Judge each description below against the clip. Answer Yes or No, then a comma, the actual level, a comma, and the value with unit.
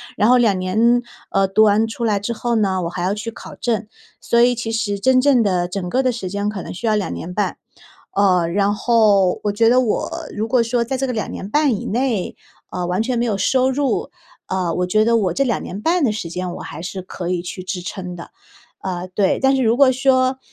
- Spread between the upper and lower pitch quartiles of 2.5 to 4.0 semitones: No, average, 4.4 semitones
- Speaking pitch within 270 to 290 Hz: No, high, 215 Hz